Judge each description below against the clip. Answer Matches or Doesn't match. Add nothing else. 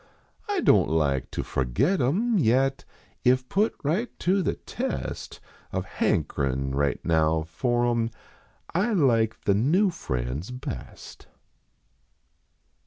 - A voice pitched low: Matches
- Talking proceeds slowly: Matches